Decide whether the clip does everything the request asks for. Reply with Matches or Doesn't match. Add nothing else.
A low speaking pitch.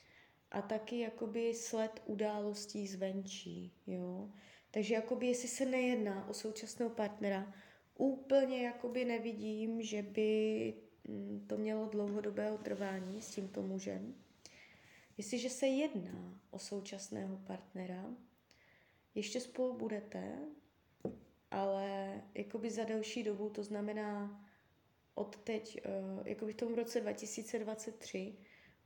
Doesn't match